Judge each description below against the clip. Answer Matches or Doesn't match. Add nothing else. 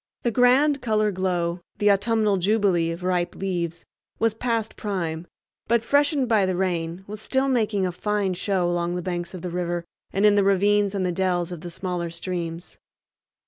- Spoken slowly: Doesn't match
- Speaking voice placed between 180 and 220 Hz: Matches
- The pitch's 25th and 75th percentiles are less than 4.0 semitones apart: Matches